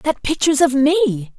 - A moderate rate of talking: No, fast, 215 wpm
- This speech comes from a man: No, female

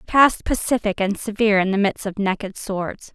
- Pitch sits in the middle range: No, high, 205 Hz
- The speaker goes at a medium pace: No, fast, 210 wpm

